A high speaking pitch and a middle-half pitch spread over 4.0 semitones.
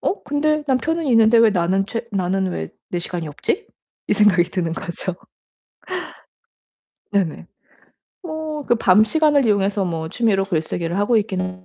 Yes: high, 200 Hz; wide, 5.5 semitones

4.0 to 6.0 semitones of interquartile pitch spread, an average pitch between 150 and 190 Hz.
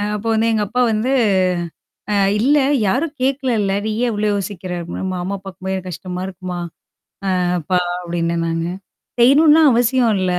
No: wide, 5.4 semitones; high, 205 Hz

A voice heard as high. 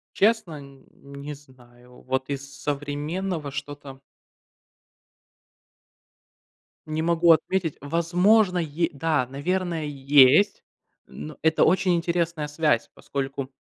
No: medium, 150 Hz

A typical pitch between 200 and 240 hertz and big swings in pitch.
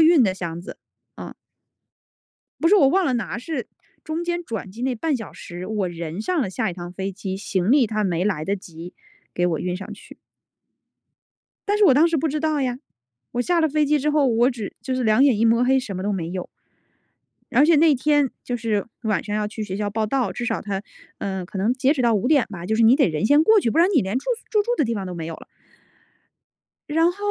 Yes: high, 230 Hz; wide, 7.2 semitones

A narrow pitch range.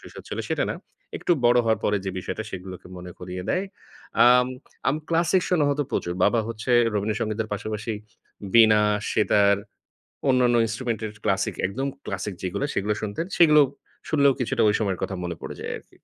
No: average, 4.1 semitones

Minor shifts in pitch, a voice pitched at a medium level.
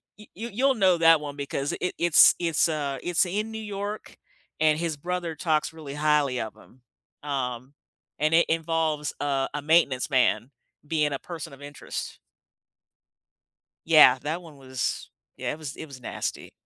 No: average, 3.3 semitones; medium, 155 Hz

